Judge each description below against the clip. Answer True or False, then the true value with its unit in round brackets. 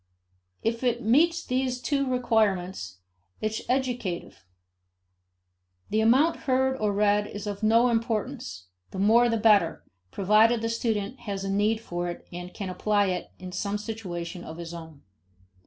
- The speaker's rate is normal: True (155 wpm)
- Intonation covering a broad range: False (4.2 semitones)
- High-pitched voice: True (215 Hz)